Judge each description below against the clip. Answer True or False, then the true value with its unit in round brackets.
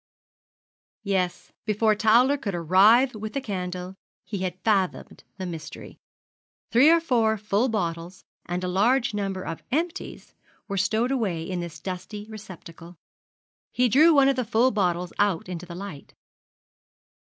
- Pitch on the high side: True (200 Hz)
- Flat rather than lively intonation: False (4.3 semitones)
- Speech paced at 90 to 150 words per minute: True (145 wpm)